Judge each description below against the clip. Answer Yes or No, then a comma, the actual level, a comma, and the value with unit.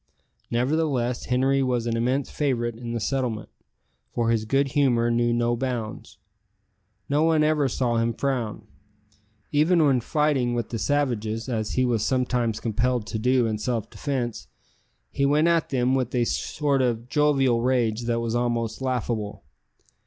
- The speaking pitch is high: No, low, 125 Hz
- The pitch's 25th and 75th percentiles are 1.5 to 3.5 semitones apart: Yes, average, 2.7 semitones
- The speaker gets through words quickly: No, average, 155 wpm